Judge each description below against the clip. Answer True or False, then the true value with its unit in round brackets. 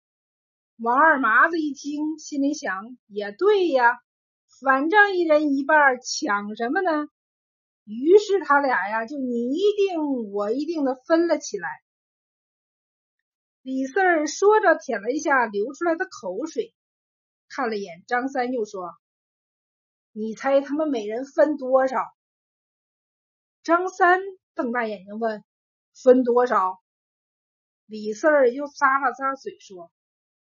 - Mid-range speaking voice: False (275 Hz)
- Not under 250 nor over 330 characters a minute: False (170 characters per minute)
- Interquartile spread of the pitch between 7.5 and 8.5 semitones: False (5.4 semitones)